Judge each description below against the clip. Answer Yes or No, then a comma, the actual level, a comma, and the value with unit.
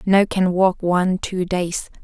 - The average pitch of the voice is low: No, medium, 185 Hz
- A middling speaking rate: Yes, average, 175 wpm